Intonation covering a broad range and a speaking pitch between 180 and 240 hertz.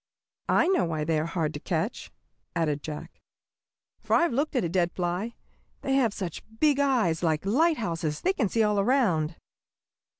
Yes: wide, 7.9 semitones; medium, 185 Hz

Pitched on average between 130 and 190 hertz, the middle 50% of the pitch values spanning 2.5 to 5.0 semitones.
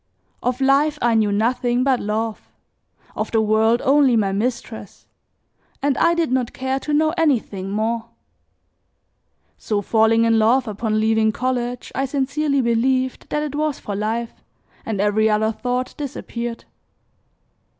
No: high, 235 Hz; average, 3.4 semitones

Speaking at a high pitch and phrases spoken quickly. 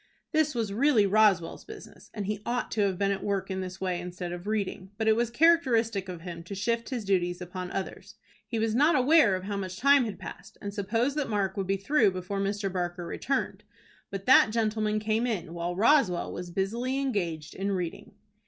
Yes: high, 200 Hz; fast, 210 wpm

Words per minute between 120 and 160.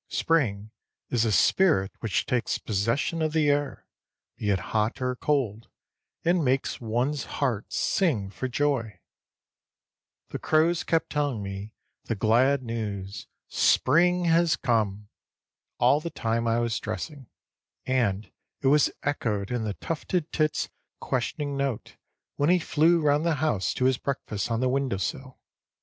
Yes: average, 145 wpm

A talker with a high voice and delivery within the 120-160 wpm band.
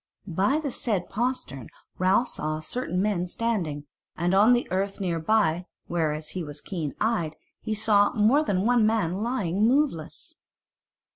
Yes: high, 195 Hz; average, 150 wpm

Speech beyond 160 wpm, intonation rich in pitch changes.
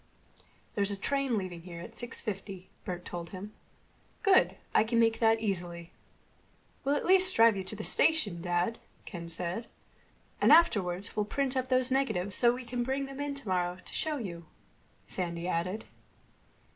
Yes: average, 170 wpm; wide, 6.3 semitones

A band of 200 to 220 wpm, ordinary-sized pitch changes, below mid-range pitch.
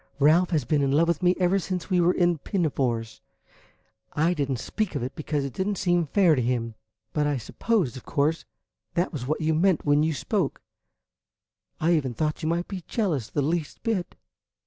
No: fast, 205 wpm; average, 4.0 semitones; medium, 155 Hz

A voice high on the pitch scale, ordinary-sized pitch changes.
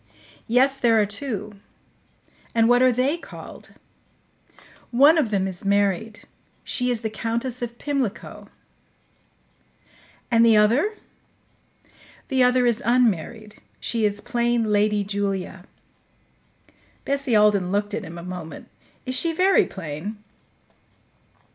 Yes: high, 225 Hz; average, 3.6 semitones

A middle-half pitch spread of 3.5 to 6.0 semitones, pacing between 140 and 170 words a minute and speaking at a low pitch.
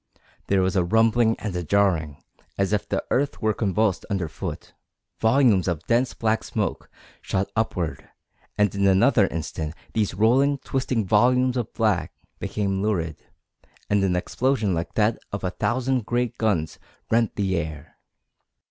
Yes: average, 4.0 semitones; average, 150 wpm; low, 105 Hz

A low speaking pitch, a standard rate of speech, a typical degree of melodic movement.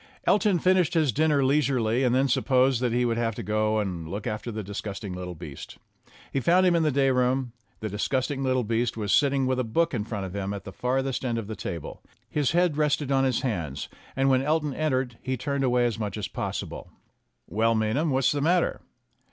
No: low, 125 Hz; fast, 220 wpm; average, 4.5 semitones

